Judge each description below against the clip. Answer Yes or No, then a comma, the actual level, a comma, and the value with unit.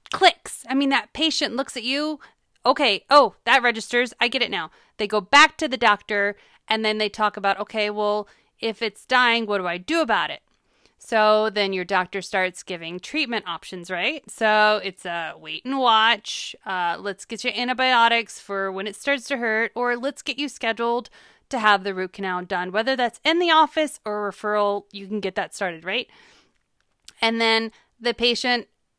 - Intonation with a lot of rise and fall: No, average, 4.0 semitones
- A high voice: Yes, high, 225 Hz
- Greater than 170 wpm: Yes, average, 195 wpm